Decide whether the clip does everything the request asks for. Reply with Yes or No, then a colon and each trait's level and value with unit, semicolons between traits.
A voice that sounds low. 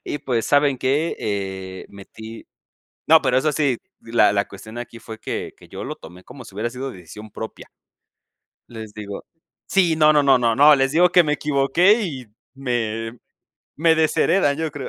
Yes: low, 130 Hz